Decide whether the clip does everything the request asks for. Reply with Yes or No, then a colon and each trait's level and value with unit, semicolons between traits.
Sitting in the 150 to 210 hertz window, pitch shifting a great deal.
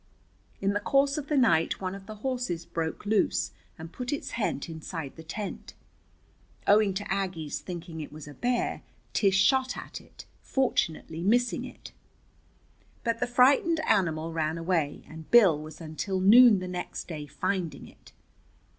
Yes: high, 190 Hz; wide, 6.7 semitones